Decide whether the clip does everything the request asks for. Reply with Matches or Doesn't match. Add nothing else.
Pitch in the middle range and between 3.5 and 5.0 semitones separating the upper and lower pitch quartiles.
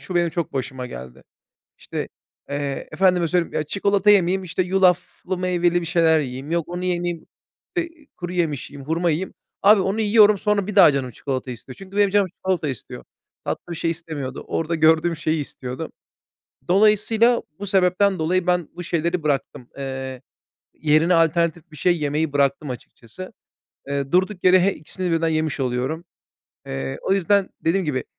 Matches